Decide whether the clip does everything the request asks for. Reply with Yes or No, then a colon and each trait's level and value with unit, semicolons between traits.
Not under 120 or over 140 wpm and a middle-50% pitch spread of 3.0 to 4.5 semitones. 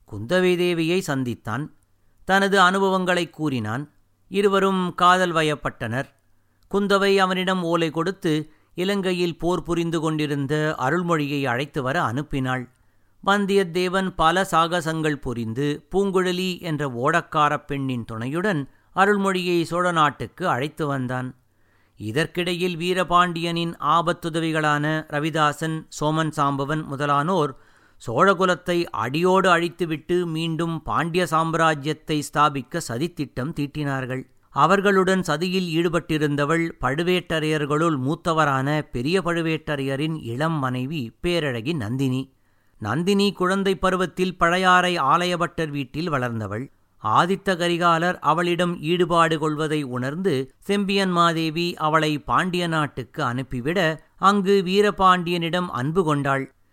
No: average, 90 wpm; average, 4.2 semitones